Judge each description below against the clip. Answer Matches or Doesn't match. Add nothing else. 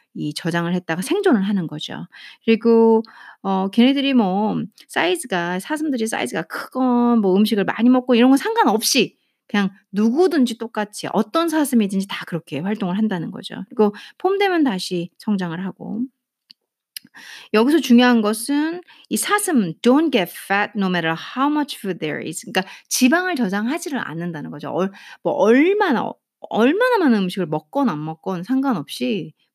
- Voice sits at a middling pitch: Doesn't match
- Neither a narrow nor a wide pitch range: Doesn't match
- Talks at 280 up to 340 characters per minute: Doesn't match